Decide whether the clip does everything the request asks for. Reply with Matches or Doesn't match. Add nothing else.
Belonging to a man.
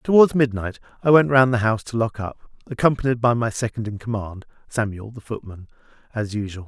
Matches